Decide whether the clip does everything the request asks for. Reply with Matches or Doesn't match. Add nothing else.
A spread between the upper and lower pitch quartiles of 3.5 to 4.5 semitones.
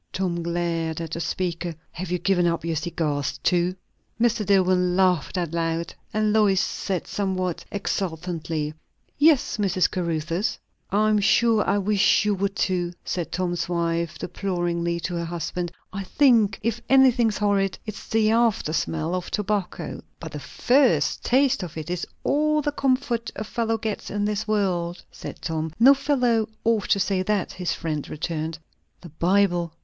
Matches